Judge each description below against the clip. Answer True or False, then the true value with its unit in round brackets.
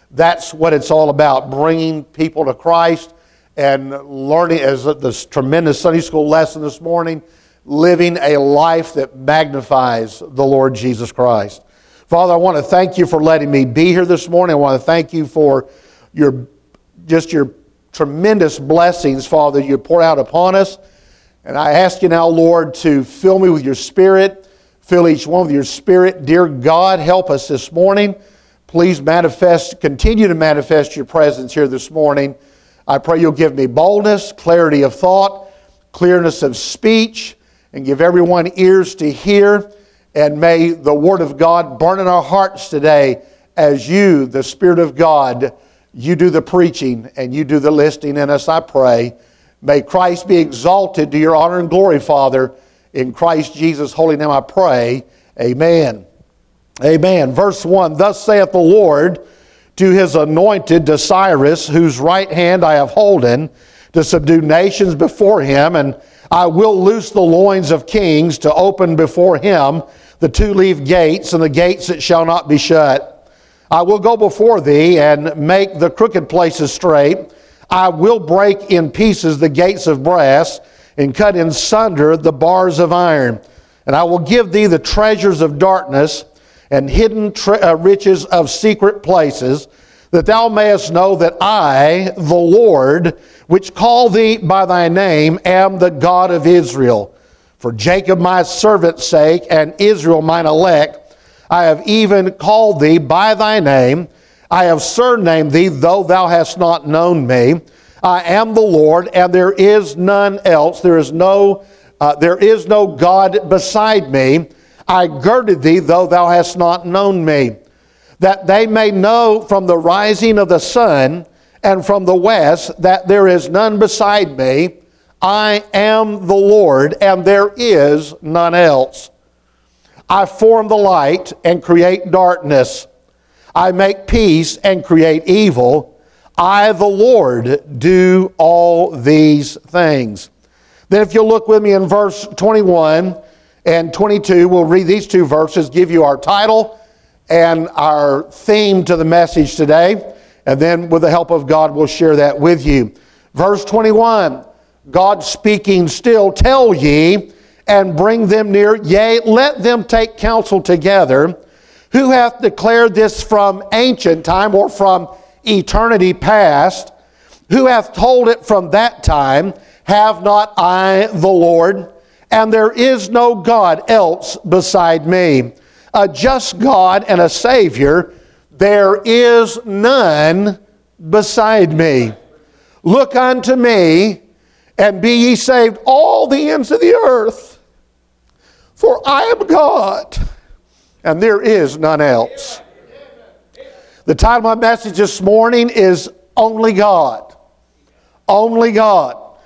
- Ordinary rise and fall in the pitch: True (4.5 semitones)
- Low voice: False (175 Hz)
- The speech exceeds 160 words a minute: False (150 wpm)